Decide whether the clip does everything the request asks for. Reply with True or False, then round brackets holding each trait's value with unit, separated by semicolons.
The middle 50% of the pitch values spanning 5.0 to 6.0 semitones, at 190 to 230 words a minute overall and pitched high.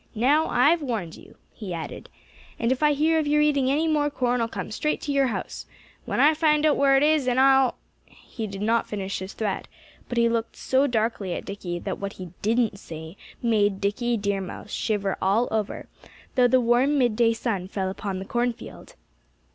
True (5.3 semitones; 205 wpm; 235 Hz)